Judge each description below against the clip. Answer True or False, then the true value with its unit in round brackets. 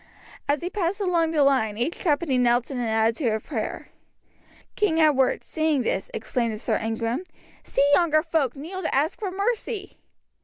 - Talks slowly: False (170 wpm)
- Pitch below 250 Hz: False (290 Hz)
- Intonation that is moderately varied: False (5.9 semitones)